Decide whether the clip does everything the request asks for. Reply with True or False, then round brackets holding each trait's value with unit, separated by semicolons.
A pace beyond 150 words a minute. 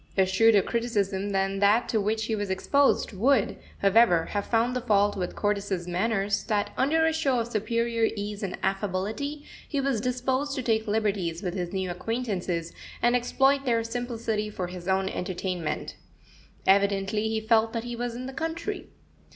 True (170 wpm)